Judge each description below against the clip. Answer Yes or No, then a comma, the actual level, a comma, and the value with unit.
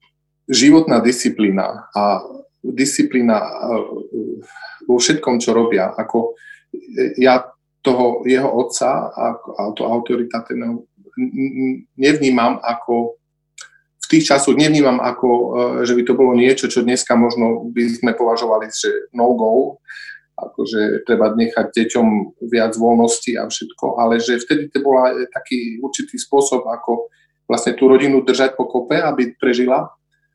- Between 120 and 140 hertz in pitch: Yes, low, 125 Hz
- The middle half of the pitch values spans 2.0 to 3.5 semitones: No, average, 4.3 semitones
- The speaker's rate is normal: Yes, average, 125 wpm